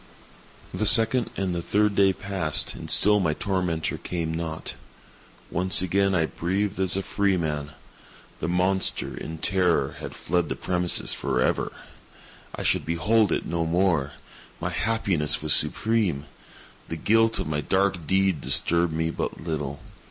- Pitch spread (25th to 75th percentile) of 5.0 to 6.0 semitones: No, average, 3.4 semitones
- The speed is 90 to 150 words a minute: Yes, average, 145 wpm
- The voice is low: Yes, very low, 90 Hz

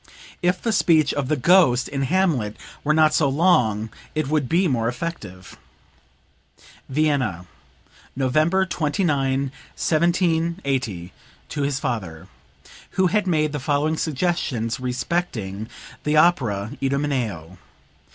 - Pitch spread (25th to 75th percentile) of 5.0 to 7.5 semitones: Yes, wide, 5.5 semitones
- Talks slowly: Yes, slow, 110 wpm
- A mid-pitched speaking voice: Yes, medium, 145 Hz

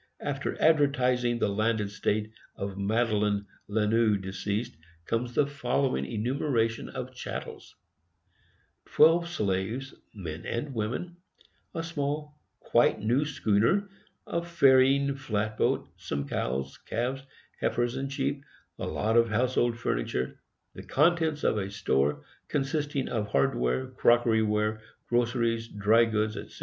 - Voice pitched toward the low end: Yes, low, 115 Hz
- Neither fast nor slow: No, slow, 120 wpm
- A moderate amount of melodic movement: Yes, average, 4.6 semitones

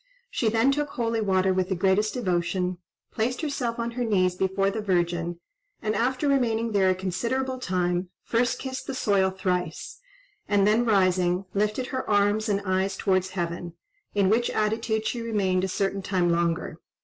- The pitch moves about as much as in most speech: Yes, average, 3.8 semitones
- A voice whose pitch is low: No, high, 200 Hz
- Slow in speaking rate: No, average, 170 wpm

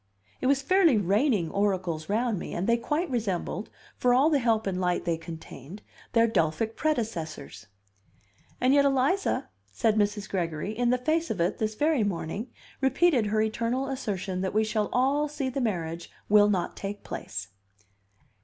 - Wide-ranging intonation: Yes, wide, 5.9 semitones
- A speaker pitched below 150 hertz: No, high, 215 Hz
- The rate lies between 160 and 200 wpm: Yes, average, 165 wpm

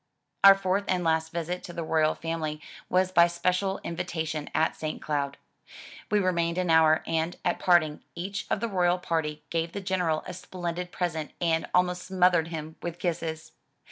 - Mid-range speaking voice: Yes, medium, 170 Hz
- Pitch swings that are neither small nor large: No, narrow, 2.2 semitones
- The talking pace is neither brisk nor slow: Yes, average, 175 wpm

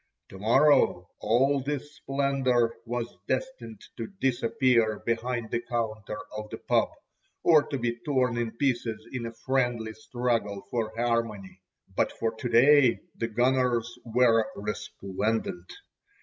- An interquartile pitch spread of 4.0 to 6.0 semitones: No, narrow, 2.5 semitones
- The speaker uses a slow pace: Yes, slow, 130 wpm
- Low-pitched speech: Yes, low, 120 Hz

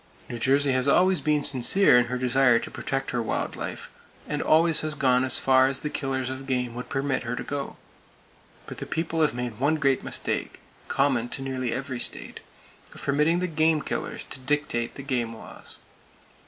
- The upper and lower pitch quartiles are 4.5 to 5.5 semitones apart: No, average, 2.8 semitones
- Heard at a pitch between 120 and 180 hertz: Yes, low, 135 Hz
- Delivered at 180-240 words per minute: Yes, average, 185 wpm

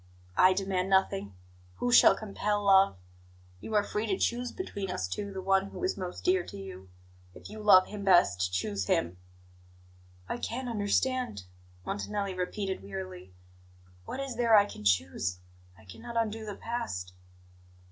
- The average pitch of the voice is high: Yes, high, 195 Hz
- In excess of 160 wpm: No, average, 155 wpm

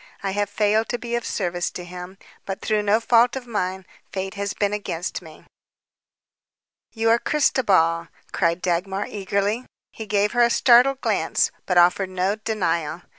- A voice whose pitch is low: No, high, 200 Hz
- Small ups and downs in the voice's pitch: No, average, 3.7 semitones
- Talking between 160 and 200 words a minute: Yes, average, 165 wpm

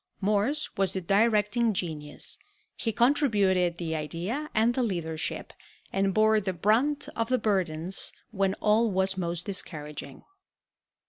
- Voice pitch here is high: Yes, high, 195 Hz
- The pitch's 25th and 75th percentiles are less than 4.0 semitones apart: No, average, 4.4 semitones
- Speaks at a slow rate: Yes, slow, 130 wpm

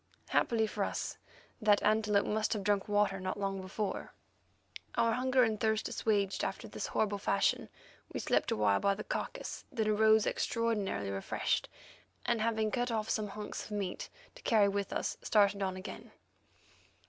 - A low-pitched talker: No, high, 210 Hz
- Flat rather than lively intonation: Yes, narrow, 1.7 semitones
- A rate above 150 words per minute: Yes, average, 160 wpm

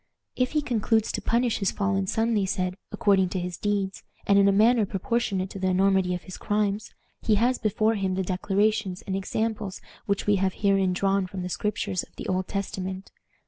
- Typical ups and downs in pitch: No, narrow, 2.2 semitones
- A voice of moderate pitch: No, high, 195 Hz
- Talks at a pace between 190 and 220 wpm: Yes, average, 200 wpm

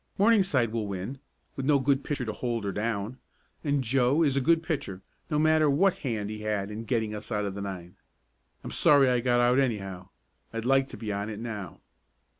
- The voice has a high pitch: No, low, 120 Hz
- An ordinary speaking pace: No, fast, 210 wpm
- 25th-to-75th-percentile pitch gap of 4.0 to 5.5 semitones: Yes, average, 4.8 semitones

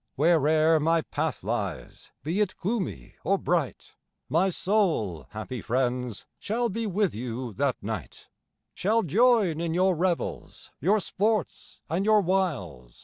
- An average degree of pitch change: No, wide, 7.7 semitones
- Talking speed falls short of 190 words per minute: Yes, slow, 135 wpm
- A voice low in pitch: No, medium, 165 Hz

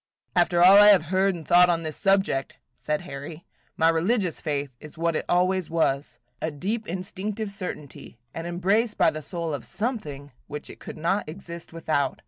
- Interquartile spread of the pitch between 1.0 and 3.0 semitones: No, average, 3.9 semitones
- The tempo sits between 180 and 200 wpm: Yes, average, 185 wpm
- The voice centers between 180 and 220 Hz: No, medium, 170 Hz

